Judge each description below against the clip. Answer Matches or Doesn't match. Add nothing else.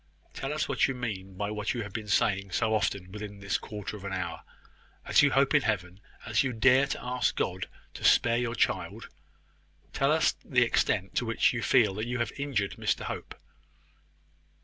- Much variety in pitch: Doesn't match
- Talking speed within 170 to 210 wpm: Matches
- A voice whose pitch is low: Matches